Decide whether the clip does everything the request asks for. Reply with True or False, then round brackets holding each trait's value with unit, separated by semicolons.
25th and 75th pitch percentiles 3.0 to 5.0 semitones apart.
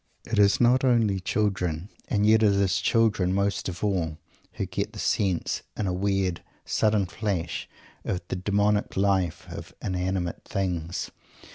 False (2.5 semitones)